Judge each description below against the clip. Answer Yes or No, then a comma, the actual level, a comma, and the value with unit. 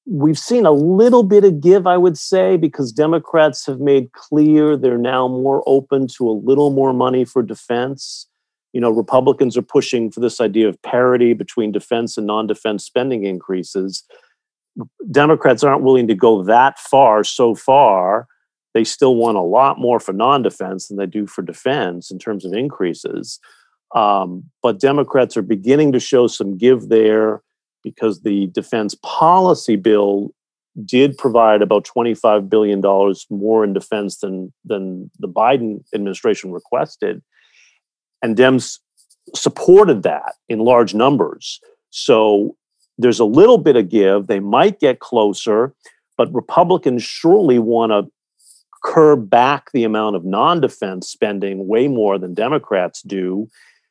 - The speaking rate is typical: Yes, average, 150 wpm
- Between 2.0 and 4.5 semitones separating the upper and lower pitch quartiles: No, average, 4.9 semitones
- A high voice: No, low, 115 Hz